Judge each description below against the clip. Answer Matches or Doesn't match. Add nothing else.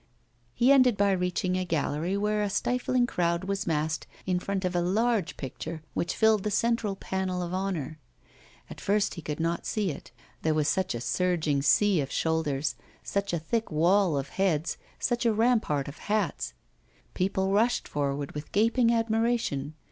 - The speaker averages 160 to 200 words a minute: Matches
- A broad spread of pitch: Doesn't match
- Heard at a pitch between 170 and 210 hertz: Matches